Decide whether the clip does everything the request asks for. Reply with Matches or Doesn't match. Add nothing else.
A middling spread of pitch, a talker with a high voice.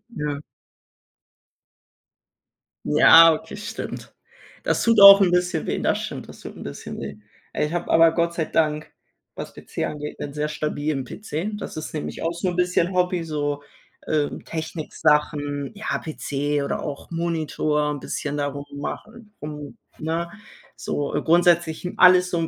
Doesn't match